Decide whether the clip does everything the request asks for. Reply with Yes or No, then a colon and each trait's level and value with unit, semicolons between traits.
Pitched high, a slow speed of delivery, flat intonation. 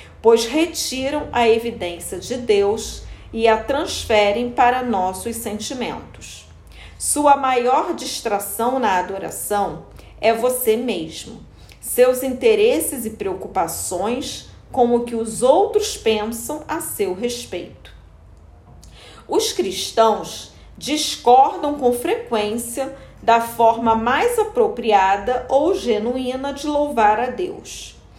No: high, 245 Hz; slow, 100 wpm; average, 4.5 semitones